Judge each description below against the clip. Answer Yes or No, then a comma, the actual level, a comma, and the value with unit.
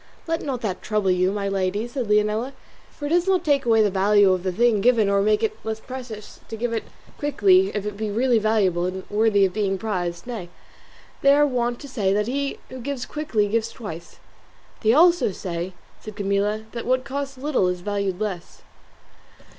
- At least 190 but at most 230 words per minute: Yes, average, 200 wpm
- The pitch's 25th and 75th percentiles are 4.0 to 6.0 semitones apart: Yes, average, 4.4 semitones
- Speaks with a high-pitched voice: Yes, high, 215 Hz